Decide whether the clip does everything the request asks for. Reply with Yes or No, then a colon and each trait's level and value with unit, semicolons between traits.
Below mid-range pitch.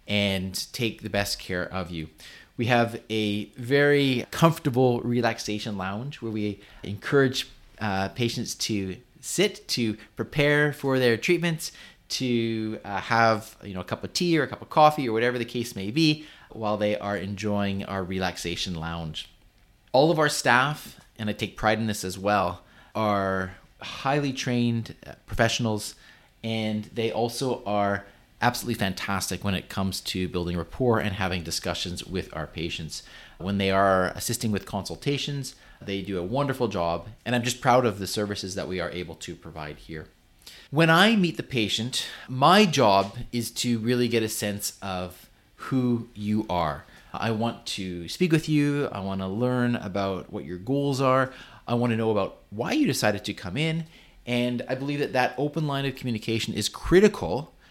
Yes: low, 110 Hz